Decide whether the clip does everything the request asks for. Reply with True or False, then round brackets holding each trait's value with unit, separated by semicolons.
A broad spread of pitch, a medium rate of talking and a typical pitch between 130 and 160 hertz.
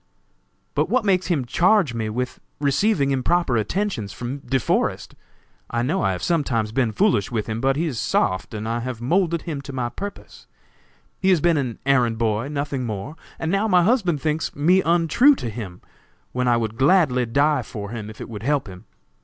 True (6.6 semitones; 195 wpm; 135 Hz)